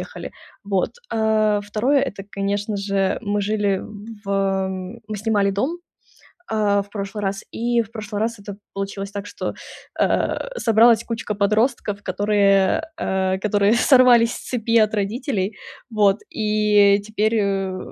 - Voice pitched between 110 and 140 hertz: No, high, 210 Hz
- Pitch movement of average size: No, narrow, 2.0 semitones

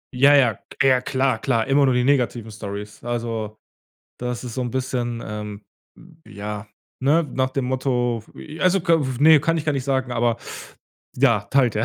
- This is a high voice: No, low, 125 Hz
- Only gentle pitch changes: No, average, 3.1 semitones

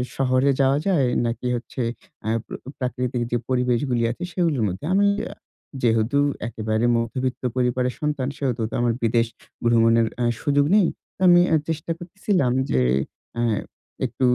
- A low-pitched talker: Yes, low, 125 Hz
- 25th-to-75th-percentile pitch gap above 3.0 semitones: Yes, average, 3.4 semitones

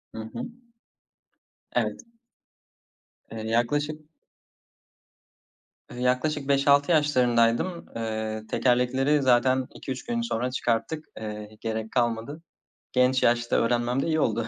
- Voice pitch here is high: No, low, 125 Hz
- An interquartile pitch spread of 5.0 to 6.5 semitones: No, average, 3.7 semitones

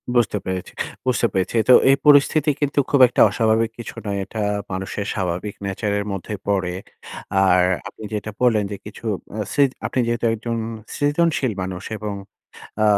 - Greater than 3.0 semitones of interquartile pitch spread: Yes, average, 4.0 semitones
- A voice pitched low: Yes, low, 110 Hz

